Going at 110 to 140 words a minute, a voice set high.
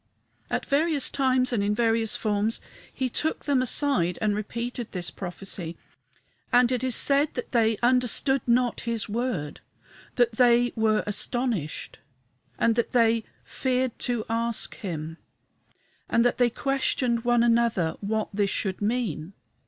Yes: slow, 135 wpm; high, 235 Hz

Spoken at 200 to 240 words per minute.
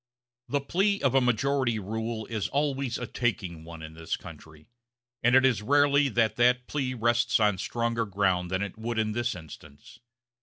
No: average, 175 wpm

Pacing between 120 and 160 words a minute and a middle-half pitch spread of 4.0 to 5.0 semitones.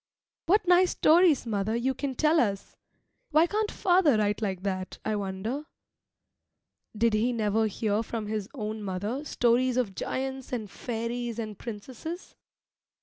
Yes: average, 145 wpm; average, 4.3 semitones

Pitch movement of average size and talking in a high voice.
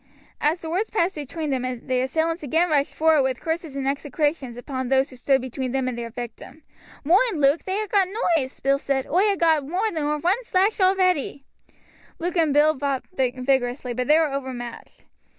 Yes: average, 4.3 semitones; very high, 290 Hz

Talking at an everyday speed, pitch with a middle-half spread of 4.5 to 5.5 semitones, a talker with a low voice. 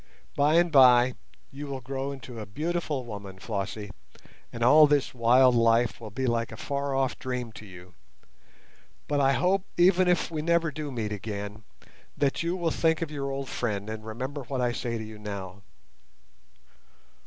Yes: average, 175 wpm; average, 4.9 semitones; low, 130 Hz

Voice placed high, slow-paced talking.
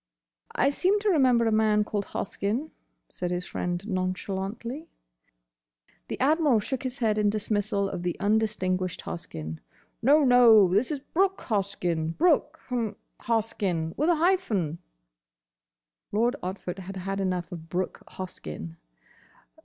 Yes: high, 210 Hz; slow, 125 wpm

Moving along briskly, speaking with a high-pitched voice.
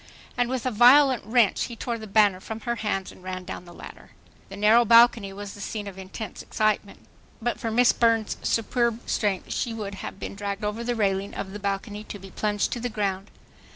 Yes: fast, 215 wpm; high, 210 Hz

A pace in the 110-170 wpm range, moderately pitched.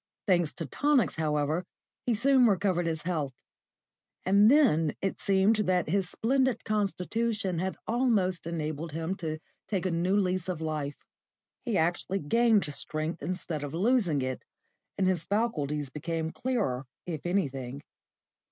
Yes: average, 140 wpm; medium, 180 Hz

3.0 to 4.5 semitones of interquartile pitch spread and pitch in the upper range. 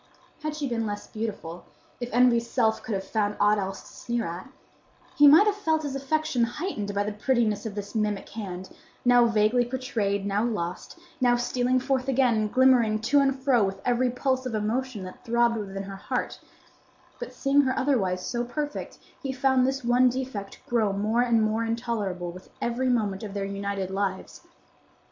Yes: average, 4.0 semitones; high, 235 Hz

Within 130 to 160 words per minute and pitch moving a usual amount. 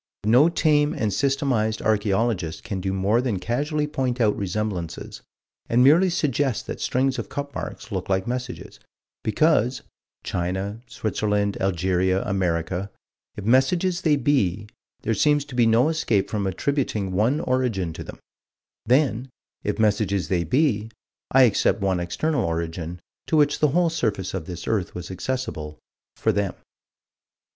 No: average, 150 wpm; wide, 6.0 semitones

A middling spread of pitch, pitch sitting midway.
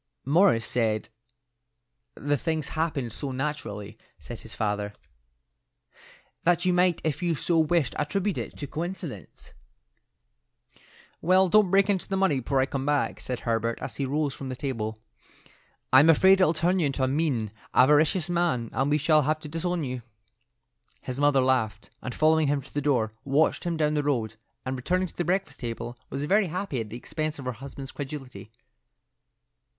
Yes: average, 4.7 semitones; medium, 145 Hz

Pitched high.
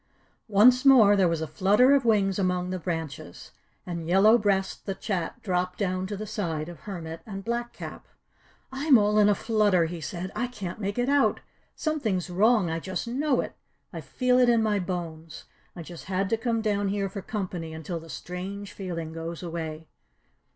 Yes: high, 195 Hz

